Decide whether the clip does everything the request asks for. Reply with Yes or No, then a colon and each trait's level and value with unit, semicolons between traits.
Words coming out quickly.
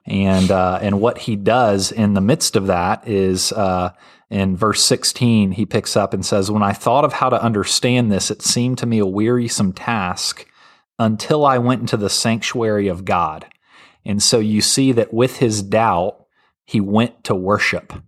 No: average, 185 wpm